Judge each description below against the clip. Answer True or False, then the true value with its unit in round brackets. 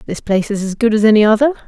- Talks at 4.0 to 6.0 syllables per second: False (7.9 syllables/s)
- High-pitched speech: True (220 Hz)